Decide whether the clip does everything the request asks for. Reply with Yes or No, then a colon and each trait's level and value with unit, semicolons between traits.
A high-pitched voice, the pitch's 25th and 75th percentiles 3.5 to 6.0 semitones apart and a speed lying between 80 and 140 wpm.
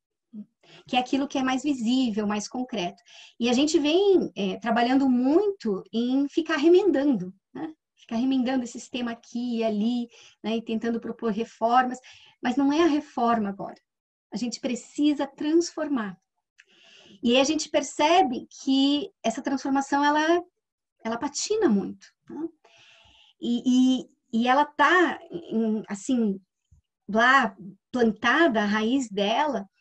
Yes: very high, 255 Hz; average, 4.6 semitones; average, 130 wpm